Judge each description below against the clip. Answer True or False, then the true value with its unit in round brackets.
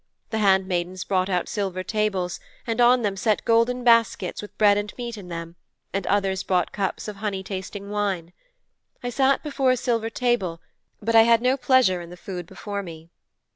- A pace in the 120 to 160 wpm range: False (185 wpm)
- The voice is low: False (205 Hz)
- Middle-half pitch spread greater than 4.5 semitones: False (3.8 semitones)